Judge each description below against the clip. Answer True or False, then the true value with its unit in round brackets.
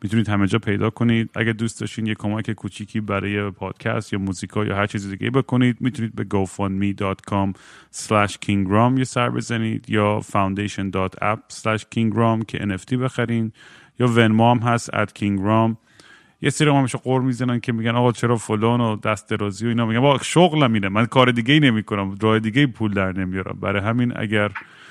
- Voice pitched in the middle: False (110 Hz)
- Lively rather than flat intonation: False (2.8 semitones)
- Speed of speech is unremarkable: False (175 wpm)